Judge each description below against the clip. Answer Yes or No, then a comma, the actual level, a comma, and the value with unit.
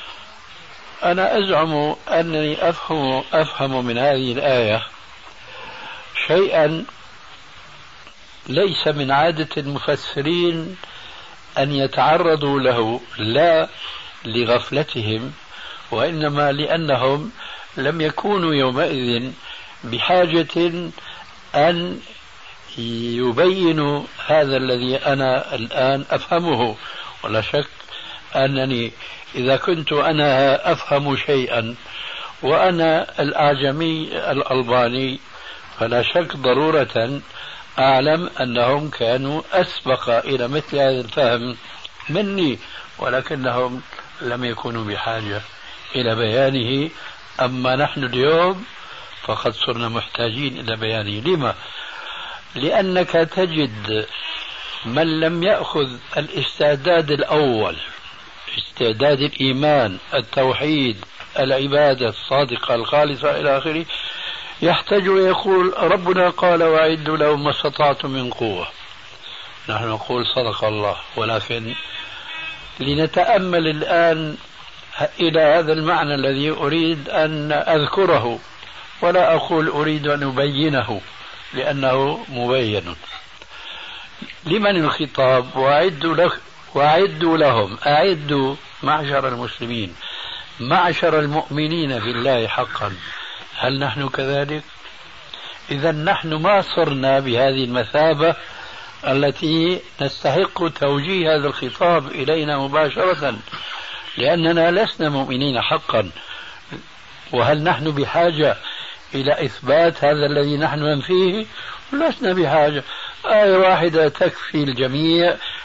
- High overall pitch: No, medium, 145 Hz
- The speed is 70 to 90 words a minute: Yes, average, 85 wpm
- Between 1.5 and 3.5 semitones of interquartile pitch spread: No, average, 4.0 semitones